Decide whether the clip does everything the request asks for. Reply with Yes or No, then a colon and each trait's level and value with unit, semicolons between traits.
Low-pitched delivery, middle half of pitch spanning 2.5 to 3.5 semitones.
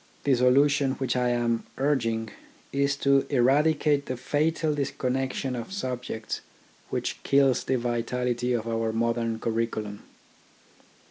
Yes: low, 125 Hz; average, 3.1 semitones